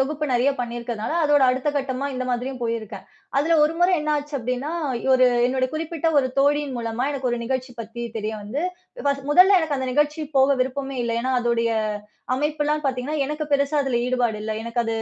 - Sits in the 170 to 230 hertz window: No, very high, 265 Hz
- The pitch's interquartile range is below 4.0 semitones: Yes, average, 3.5 semitones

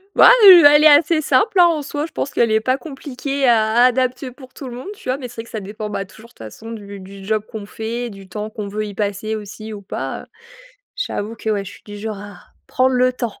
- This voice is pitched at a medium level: No, high, 225 Hz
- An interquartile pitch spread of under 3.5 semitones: No, average, 4.1 semitones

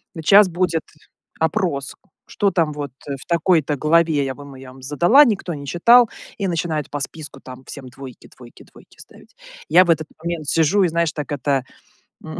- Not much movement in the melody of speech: No, average, 3.6 semitones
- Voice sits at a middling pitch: Yes, medium, 155 Hz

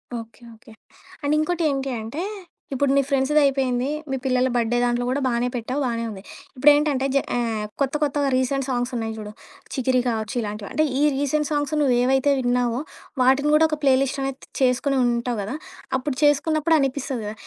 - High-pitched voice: Yes, very high, 260 Hz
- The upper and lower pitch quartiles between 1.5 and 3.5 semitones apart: Yes, average, 2.8 semitones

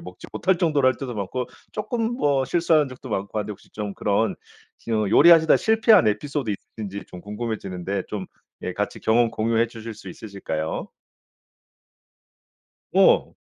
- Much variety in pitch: Yes, wide, 6.1 semitones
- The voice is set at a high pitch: No, low, 115 Hz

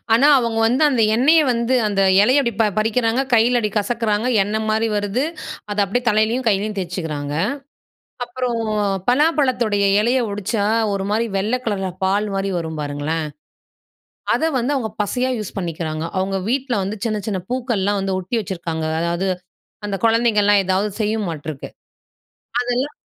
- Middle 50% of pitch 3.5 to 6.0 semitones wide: Yes, average, 3.8 semitones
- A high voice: Yes, high, 215 Hz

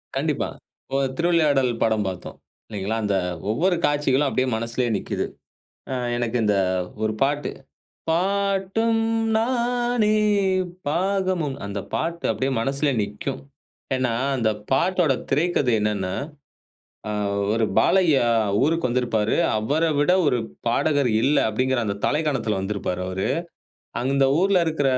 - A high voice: No, low, 135 Hz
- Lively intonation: Yes, wide, 7.0 semitones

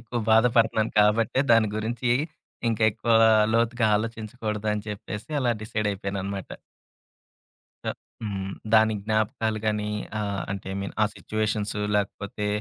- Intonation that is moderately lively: No, narrow, 1.5 semitones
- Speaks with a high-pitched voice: No, low, 110 Hz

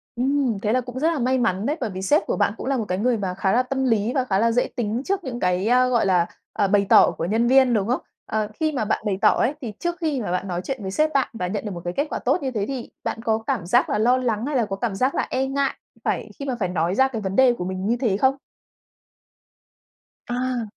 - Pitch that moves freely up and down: No, average, 4.7 semitones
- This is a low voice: No, high, 235 Hz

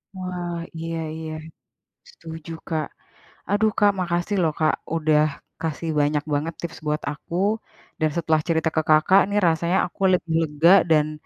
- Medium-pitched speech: Yes, medium, 165 Hz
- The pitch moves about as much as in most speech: No, narrow, 2.3 semitones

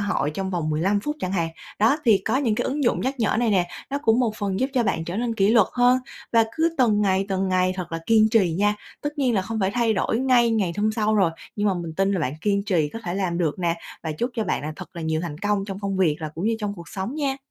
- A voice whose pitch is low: No, high, 200 Hz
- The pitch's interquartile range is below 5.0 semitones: Yes, average, 4.2 semitones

